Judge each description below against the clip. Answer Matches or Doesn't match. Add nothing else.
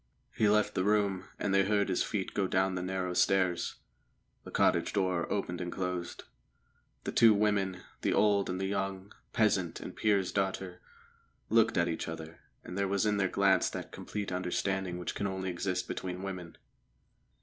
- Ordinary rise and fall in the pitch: Doesn't match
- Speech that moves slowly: Doesn't match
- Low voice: Matches